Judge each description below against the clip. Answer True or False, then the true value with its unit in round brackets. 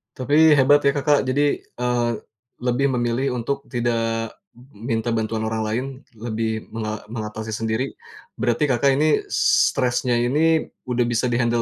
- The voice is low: True (120 Hz)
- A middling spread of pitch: True (3.1 semitones)